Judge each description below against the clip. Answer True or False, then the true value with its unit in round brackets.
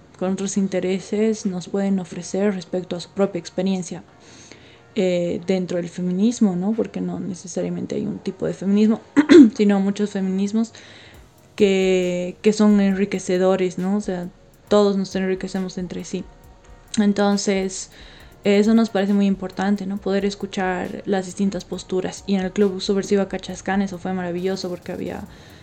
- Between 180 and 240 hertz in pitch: True (190 Hz)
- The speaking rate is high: False (145 wpm)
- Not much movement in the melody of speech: True (1.6 semitones)